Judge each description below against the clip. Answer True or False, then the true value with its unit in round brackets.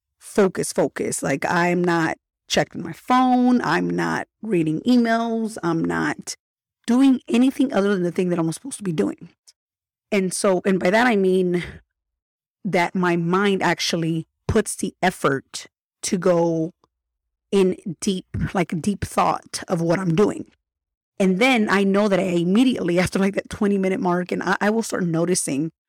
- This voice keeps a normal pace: True (160 wpm)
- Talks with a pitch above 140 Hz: True (190 Hz)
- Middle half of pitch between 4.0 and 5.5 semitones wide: False (3.6 semitones)